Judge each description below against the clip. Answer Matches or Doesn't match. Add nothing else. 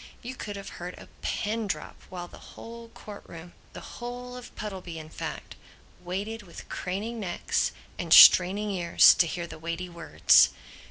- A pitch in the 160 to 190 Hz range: Matches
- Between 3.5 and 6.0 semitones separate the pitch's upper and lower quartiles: Matches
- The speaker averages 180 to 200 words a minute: Doesn't match